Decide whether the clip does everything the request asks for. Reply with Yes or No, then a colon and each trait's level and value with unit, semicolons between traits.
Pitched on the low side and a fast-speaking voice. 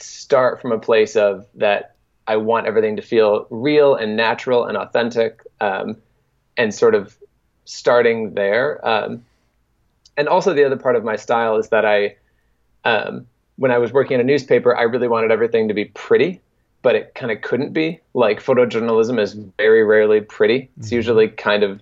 No: low, 115 Hz; average, 180 wpm